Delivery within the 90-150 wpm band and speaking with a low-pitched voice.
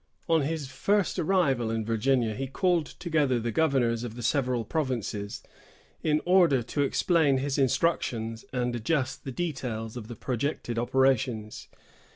Yes: average, 145 wpm; low, 130 Hz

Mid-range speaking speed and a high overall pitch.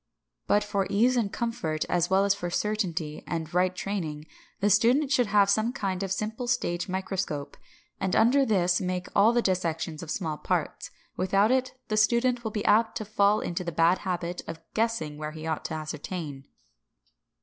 Yes: average, 180 wpm; high, 195 Hz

